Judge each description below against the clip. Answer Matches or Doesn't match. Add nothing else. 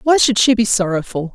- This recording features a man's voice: Doesn't match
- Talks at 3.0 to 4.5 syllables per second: Doesn't match